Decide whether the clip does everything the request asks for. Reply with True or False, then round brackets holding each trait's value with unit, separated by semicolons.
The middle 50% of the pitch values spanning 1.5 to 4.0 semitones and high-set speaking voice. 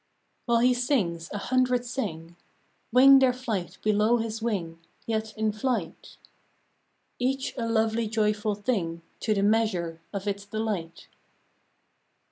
True (3.4 semitones; 220 Hz)